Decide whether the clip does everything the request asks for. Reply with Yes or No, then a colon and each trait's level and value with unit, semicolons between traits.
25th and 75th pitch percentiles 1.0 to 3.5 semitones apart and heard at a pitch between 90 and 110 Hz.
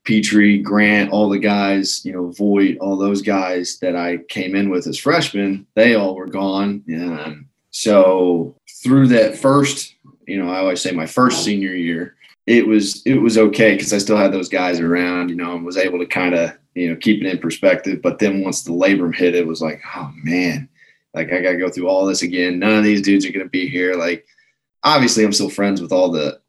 Yes: average, 2.9 semitones; very low, 95 Hz